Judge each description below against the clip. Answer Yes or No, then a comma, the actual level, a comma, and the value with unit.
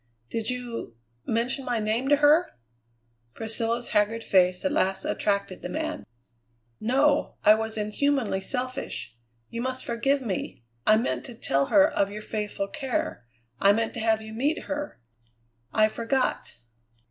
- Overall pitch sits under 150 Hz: No, high, 230 Hz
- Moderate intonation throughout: Yes, average, 4.1 semitones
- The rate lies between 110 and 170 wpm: Yes, average, 145 wpm